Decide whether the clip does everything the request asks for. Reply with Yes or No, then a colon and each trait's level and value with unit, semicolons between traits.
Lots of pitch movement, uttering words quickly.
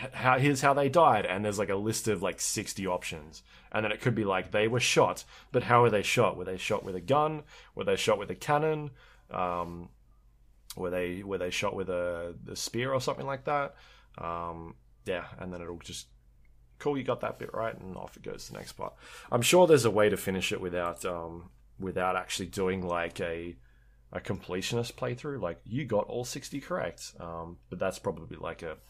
Yes: wide, 6.8 semitones; fast, 215 wpm